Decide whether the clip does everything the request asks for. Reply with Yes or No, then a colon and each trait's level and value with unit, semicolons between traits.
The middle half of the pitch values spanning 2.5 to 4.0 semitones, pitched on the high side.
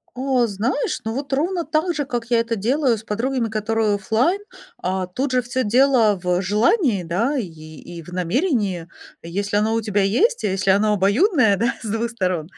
No: average, 4.7 semitones; high, 225 Hz